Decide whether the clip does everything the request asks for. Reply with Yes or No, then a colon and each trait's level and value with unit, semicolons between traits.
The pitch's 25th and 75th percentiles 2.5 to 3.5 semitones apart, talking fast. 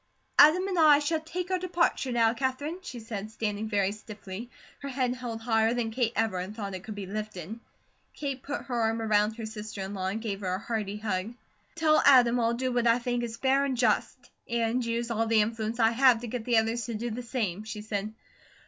Yes: average, 2.8 semitones; fast, 225 wpm